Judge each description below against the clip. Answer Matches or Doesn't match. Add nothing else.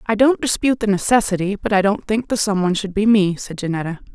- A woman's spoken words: Matches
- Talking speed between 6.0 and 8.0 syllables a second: Matches